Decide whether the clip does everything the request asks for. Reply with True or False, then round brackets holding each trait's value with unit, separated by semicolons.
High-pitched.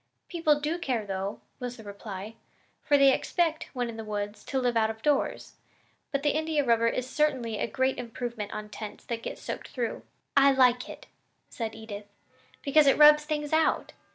True (250 Hz)